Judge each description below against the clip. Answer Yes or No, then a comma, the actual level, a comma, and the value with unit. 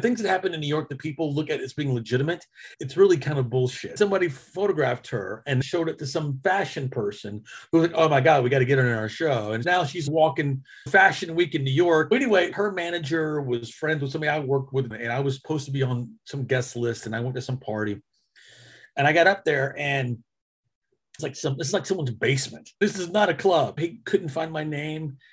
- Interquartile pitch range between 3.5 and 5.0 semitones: Yes, average, 4.4 semitones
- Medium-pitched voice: Yes, medium, 150 Hz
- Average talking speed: No, fast, 235 wpm